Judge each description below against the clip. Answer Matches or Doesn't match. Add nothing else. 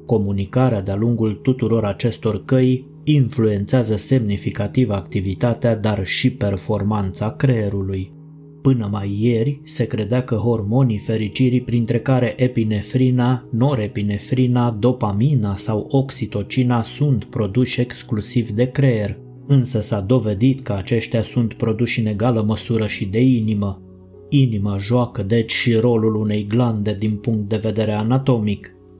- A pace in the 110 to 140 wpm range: Matches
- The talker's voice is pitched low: Matches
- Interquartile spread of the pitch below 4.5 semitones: Matches